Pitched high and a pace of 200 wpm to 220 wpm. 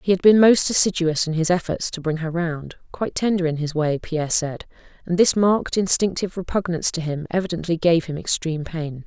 No: medium, 170 Hz; fast, 205 wpm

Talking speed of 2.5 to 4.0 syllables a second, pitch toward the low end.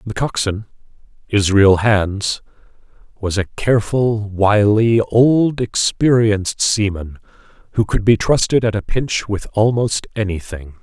Yes: 3.9 syllables/s; low, 105 Hz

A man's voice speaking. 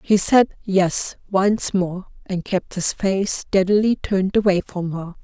No: female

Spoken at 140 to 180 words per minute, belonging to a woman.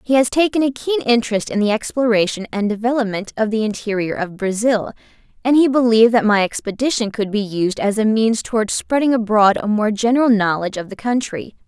No: average, 195 wpm; female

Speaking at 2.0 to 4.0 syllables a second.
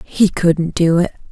Yes: 3.8 syllables/s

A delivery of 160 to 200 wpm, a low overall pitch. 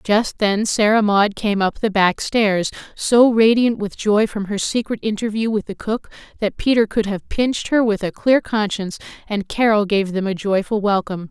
No: average, 195 wpm; high, 210 Hz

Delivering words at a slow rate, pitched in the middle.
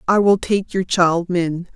No: fast, 205 wpm; medium, 180 Hz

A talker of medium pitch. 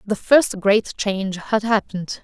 No: high, 205 Hz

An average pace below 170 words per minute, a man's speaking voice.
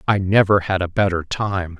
No: average, 200 wpm; male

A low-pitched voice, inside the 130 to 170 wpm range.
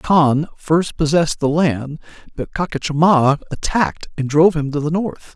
No: medium, 155 Hz; average, 155 wpm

